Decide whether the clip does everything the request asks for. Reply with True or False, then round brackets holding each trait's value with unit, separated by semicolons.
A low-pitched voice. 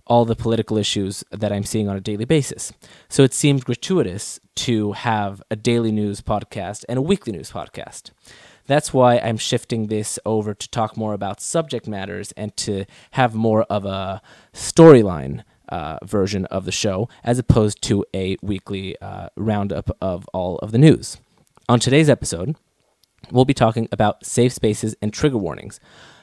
True (110 Hz)